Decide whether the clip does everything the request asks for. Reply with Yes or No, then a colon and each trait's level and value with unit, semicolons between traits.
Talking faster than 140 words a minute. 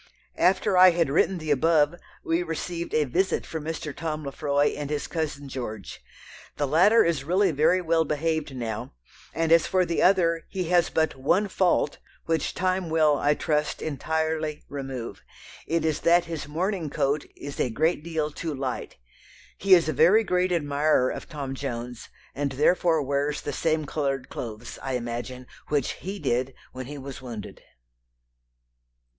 Yes: average, 165 wpm